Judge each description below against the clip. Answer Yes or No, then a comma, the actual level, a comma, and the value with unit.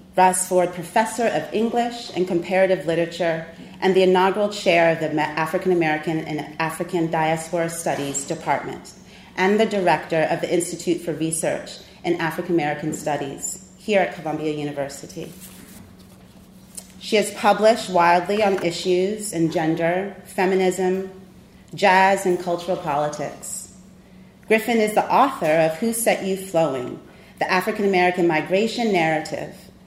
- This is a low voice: No, medium, 180 Hz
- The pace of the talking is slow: Yes, slow, 130 wpm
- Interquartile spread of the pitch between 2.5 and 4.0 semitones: Yes, average, 2.8 semitones